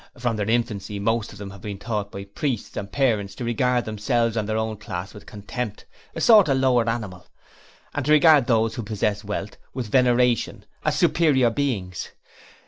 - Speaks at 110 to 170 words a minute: No, average, 185 wpm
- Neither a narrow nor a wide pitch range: Yes, average, 3.3 semitones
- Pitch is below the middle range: Yes, low, 115 Hz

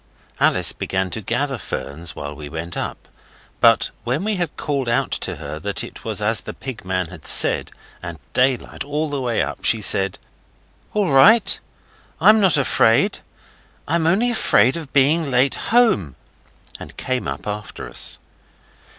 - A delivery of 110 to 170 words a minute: Yes, average, 160 wpm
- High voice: No, low, 125 Hz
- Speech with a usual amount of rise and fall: No, wide, 8.9 semitones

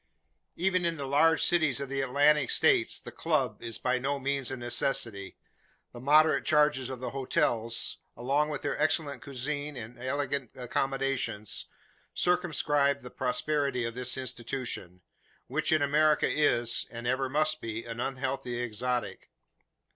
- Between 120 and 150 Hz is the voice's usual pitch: Yes, low, 135 Hz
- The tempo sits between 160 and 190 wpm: No, average, 145 wpm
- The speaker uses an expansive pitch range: No, average, 3.2 semitones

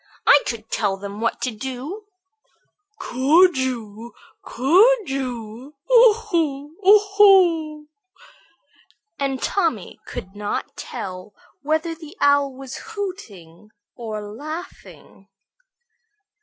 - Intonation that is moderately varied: No, wide, 7.4 semitones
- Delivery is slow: Yes, slow, 100 wpm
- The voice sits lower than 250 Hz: No, very high, 275 Hz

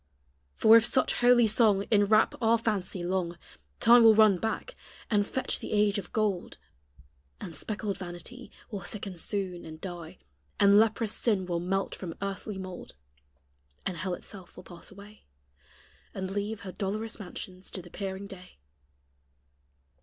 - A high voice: Yes, high, 200 Hz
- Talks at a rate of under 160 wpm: Yes, average, 150 wpm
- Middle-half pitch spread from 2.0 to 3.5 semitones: Yes, average, 2.9 semitones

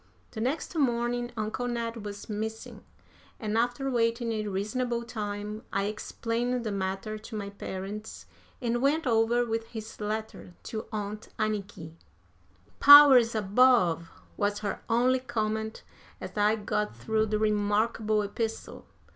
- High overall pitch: Yes, high, 220 Hz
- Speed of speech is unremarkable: No, slow, 130 wpm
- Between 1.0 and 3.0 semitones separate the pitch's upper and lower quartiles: Yes, narrow, 2.4 semitones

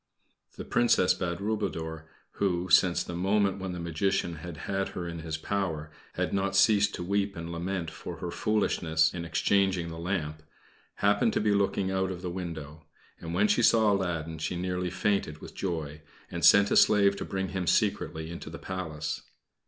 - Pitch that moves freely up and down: No, average, 3.0 semitones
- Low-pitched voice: Yes, very low, 90 Hz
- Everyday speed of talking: Yes, average, 180 wpm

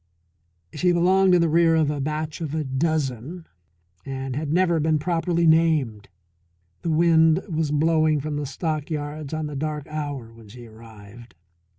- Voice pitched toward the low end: No, medium, 155 Hz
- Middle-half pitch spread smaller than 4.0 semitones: Yes, average, 3.0 semitones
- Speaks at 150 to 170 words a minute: Yes, average, 160 wpm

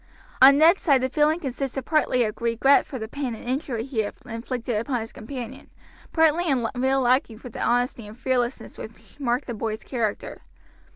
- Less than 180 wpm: No, average, 185 wpm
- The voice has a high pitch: Yes, very high, 250 Hz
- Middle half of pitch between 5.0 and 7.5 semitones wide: No, average, 3.0 semitones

